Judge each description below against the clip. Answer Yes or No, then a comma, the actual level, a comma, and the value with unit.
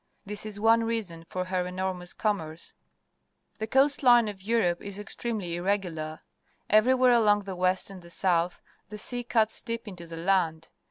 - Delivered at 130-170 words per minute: Yes, average, 165 wpm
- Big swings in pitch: No, average, 4.0 semitones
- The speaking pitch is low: No, high, 195 Hz